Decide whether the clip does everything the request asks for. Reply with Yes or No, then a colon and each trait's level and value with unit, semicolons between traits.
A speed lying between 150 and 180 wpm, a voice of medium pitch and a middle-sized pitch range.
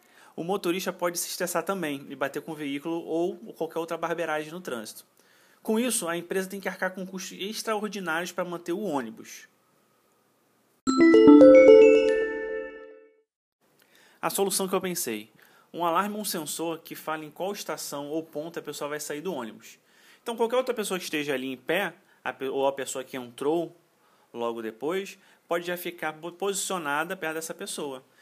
Yes: average, 165 wpm; medium, 170 Hz; average, 4.3 semitones